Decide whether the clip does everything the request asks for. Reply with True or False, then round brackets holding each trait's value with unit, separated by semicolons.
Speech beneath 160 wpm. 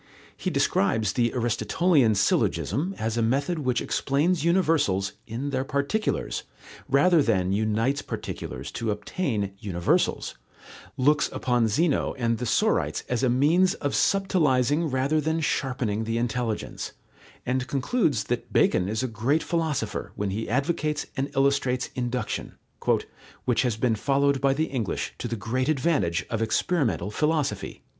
True (140 wpm)